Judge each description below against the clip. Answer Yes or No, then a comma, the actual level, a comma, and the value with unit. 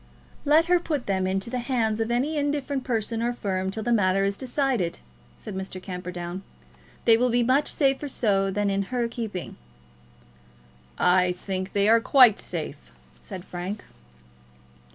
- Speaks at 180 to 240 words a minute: No, average, 155 wpm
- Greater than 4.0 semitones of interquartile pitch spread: Yes, average, 4.8 semitones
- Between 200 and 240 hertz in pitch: Yes, high, 220 Hz